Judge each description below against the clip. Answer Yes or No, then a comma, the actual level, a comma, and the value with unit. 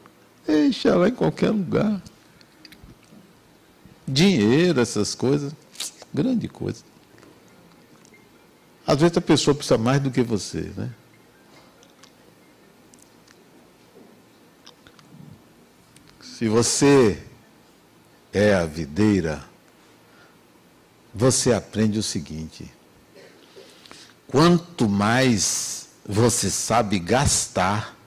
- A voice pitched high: No, low, 120 Hz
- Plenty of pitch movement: Yes, wide, 7.1 semitones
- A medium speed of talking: No, slow, 75 wpm